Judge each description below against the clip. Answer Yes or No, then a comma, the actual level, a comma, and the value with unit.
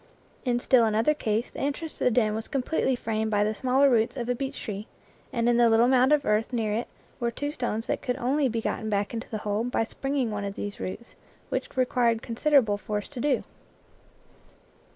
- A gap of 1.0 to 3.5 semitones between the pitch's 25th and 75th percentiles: Yes, average, 3.1 semitones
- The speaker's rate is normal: No, fast, 215 wpm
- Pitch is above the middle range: Yes, high, 235 Hz